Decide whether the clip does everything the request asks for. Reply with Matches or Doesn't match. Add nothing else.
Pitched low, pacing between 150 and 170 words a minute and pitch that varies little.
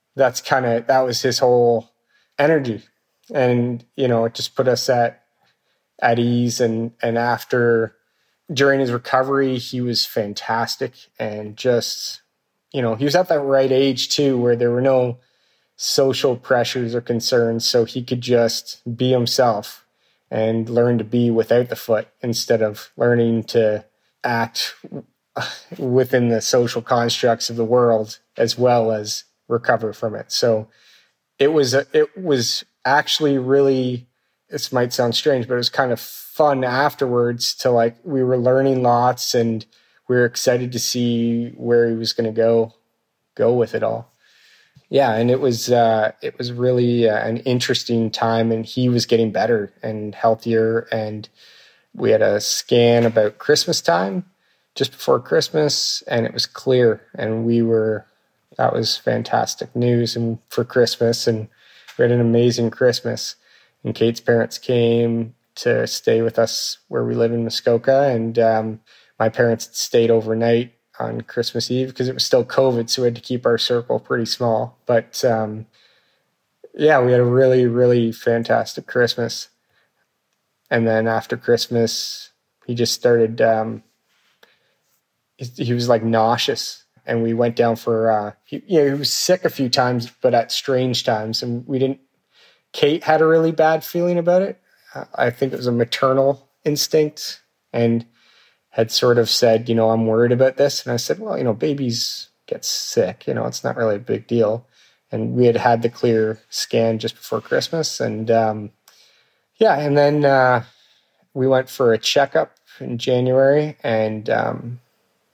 Matches